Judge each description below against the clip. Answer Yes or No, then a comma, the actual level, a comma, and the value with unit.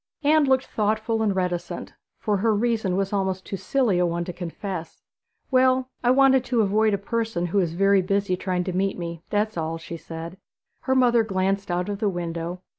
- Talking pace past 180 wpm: Yes, average, 195 wpm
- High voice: Yes, high, 195 Hz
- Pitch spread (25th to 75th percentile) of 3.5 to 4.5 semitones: Yes, average, 3.9 semitones